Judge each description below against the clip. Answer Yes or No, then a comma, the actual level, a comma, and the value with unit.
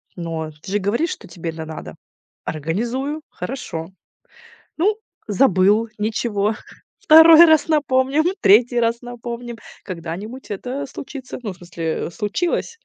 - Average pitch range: No, wide, 6.4 semitones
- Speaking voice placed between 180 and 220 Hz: No, high, 230 Hz